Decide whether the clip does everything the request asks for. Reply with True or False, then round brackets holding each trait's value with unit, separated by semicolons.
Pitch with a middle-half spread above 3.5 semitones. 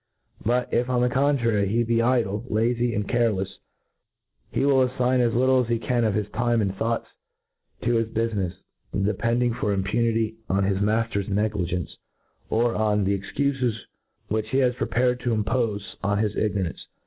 False (2.9 semitones)